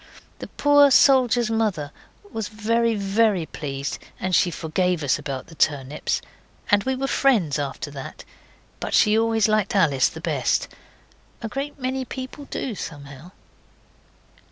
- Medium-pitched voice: No, high, 205 Hz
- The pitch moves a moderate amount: No, wide, 7.9 semitones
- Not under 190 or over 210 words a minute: No, average, 140 wpm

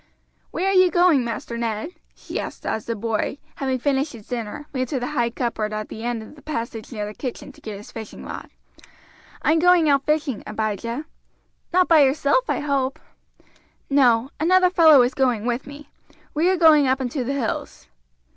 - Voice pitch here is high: Yes, very high, 265 Hz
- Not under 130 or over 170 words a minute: No, average, 195 wpm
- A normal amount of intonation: Yes, average, 4.7 semitones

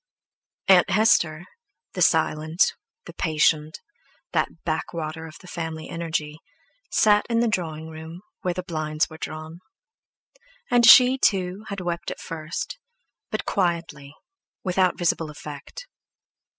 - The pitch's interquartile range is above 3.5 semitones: No, average, 2.9 semitones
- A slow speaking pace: Yes, slow, 125 wpm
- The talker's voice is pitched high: No, medium, 165 Hz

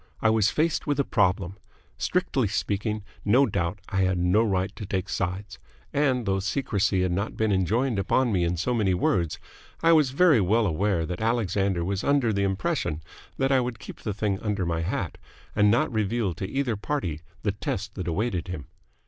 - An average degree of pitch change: Yes, average, 4.1 semitones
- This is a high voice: No, low, 100 Hz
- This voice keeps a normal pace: Yes, average, 190 wpm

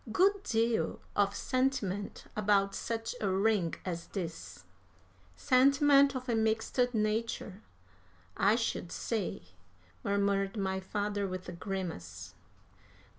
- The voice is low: No, high, 205 Hz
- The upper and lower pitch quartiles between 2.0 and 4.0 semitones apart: Yes, average, 3.2 semitones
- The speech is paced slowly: Yes, slow, 110 wpm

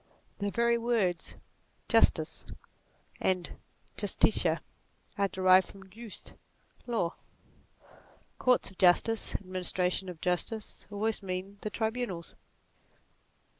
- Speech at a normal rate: No, slow, 95 wpm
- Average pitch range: Yes, average, 3.5 semitones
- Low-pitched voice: No, high, 195 Hz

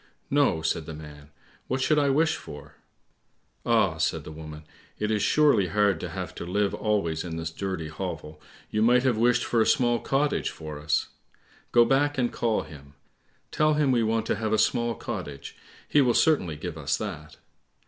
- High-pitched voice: No, low, 105 Hz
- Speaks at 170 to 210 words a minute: Yes, average, 190 wpm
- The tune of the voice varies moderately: No, wide, 7.7 semitones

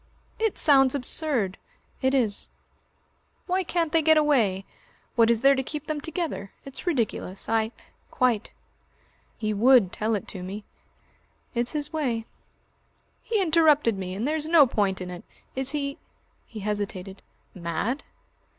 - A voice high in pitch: Yes, very high, 250 Hz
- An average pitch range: No, wide, 6.5 semitones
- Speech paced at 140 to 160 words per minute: Yes, average, 150 wpm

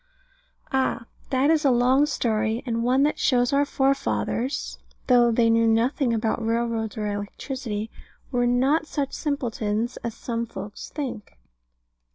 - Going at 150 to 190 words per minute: No, average, 140 wpm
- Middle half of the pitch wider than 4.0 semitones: No, average, 3.1 semitones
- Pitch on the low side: No, high, 240 Hz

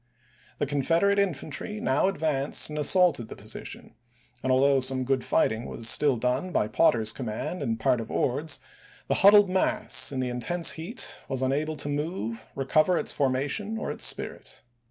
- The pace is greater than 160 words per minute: Yes, average, 175 wpm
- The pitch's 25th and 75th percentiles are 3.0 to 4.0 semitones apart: No, average, 4.8 semitones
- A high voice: No, medium, 140 Hz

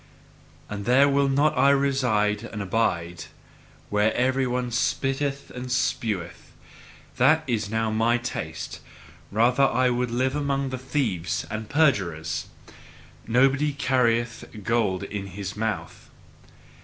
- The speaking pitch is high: No, low, 120 Hz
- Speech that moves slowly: Yes, slow, 120 wpm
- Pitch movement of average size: Yes, average, 4.3 semitones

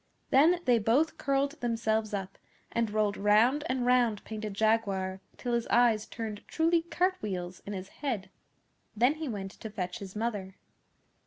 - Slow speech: No, average, 160 wpm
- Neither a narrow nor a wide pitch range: Yes, average, 3.8 semitones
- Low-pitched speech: No, high, 220 Hz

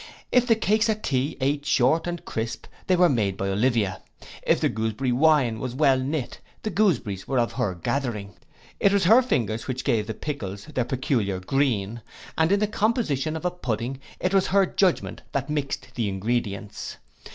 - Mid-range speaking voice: No, low, 130 Hz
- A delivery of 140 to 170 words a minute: No, average, 185 wpm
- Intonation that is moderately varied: No, wide, 7.3 semitones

